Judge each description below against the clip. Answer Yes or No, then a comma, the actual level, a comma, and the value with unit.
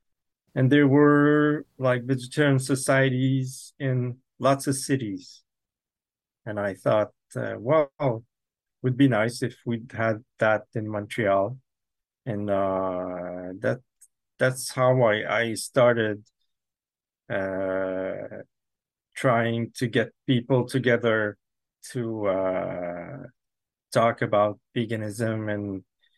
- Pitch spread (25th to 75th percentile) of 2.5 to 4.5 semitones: Yes, average, 4.2 semitones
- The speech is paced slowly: Yes, slow, 100 wpm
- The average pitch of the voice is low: Yes, low, 120 Hz